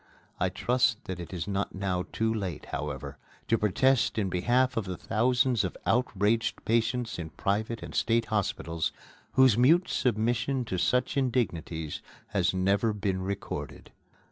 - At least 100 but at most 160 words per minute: Yes, average, 145 wpm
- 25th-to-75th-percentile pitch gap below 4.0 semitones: No, average, 4.6 semitones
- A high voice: No, low, 105 Hz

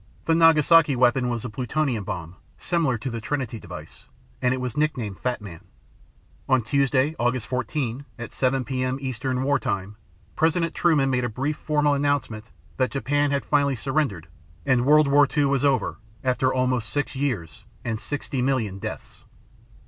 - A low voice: Yes, low, 130 Hz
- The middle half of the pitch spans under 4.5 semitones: Yes, average, 3.2 semitones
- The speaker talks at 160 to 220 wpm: Yes, average, 165 wpm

